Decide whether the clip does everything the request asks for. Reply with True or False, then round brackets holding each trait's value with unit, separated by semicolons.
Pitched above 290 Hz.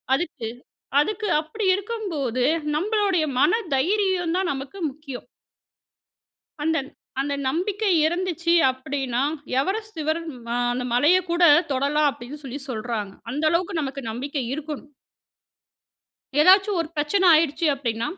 True (310 Hz)